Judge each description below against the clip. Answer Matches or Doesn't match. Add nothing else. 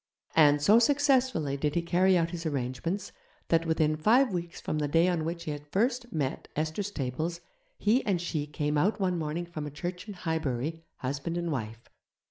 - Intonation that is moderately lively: Matches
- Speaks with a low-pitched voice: Doesn't match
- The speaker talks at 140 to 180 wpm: Doesn't match